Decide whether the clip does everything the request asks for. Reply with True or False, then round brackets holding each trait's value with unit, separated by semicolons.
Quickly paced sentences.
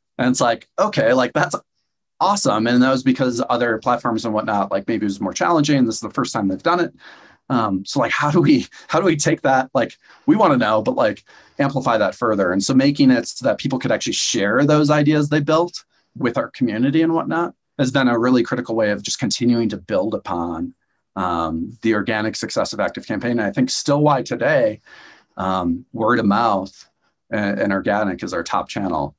True (215 wpm)